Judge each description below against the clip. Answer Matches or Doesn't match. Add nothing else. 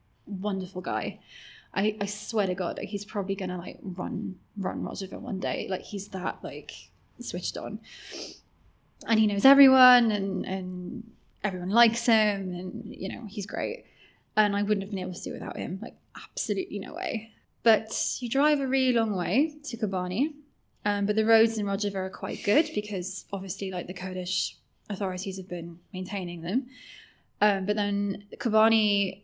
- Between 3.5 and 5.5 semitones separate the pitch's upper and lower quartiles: Doesn't match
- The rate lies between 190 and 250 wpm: Doesn't match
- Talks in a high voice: Matches